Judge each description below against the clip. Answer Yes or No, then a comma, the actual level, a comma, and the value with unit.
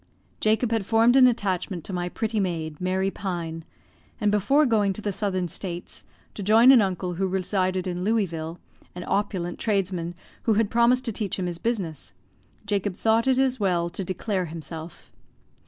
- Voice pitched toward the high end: Yes, high, 195 Hz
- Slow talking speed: No, average, 170 wpm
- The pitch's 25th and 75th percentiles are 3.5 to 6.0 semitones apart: Yes, average, 3.8 semitones